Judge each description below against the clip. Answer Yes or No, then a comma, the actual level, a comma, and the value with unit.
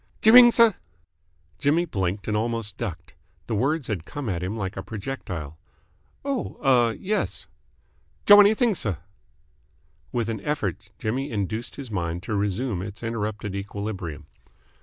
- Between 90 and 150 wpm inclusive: Yes, average, 145 wpm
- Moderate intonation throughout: No, wide, 5.9 semitones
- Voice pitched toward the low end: Yes, low, 110 Hz